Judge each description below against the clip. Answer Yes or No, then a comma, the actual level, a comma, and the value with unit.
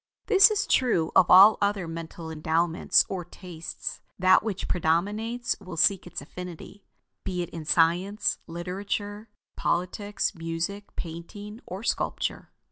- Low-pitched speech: No, medium, 180 Hz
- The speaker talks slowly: Yes, slow, 125 wpm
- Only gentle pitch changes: No, average, 3.6 semitones